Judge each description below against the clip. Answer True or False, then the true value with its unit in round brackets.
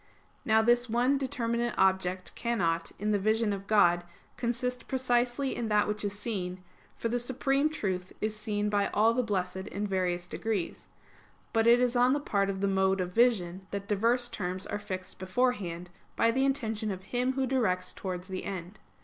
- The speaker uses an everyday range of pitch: True (4.3 semitones)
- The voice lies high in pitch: True (210 Hz)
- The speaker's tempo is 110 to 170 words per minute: False (185 wpm)